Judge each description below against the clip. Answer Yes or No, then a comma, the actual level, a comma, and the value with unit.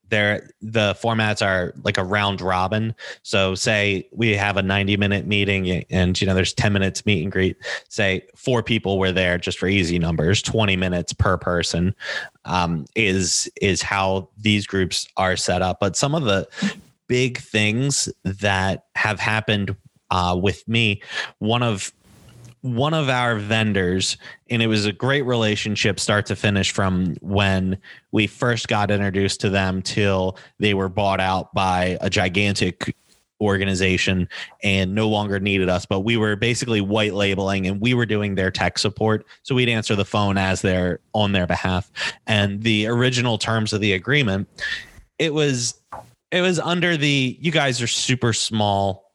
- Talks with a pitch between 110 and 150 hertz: No, low, 100 Hz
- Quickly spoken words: No, average, 165 wpm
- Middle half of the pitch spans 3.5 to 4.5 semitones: No, average, 2.9 semitones